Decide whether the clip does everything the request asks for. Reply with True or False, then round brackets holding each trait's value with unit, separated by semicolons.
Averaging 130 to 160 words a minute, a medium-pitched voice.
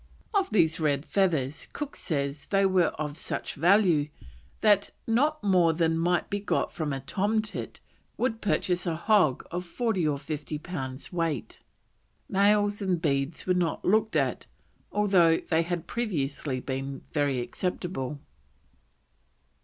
True (140 wpm; 170 Hz)